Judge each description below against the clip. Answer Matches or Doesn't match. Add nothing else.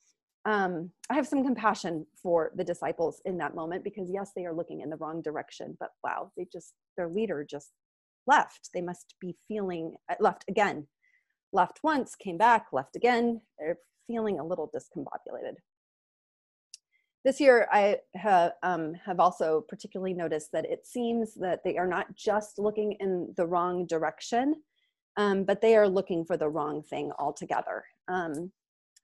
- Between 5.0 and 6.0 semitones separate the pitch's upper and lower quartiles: Matches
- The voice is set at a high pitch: Matches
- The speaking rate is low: Doesn't match